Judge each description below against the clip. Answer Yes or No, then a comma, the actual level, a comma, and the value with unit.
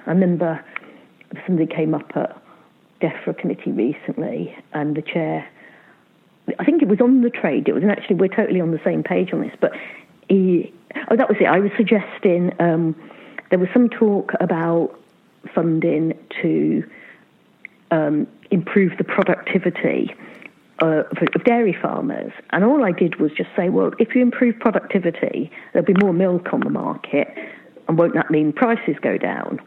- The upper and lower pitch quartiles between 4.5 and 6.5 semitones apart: Yes, average, 5.0 semitones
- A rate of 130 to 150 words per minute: No, average, 170 wpm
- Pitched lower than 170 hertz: No, medium, 185 Hz